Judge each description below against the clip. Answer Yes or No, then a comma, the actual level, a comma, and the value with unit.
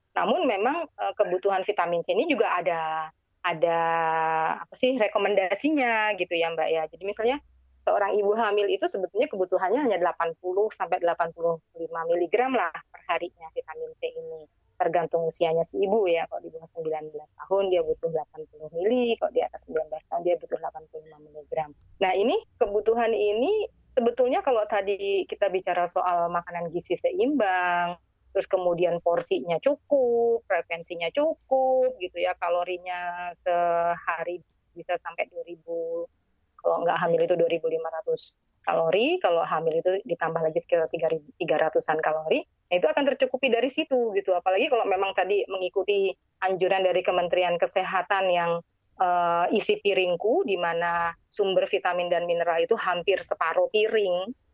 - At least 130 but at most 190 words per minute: Yes, fast, 140 wpm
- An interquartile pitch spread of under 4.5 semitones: No, average, 5.2 semitones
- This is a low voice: No, medium, 180 Hz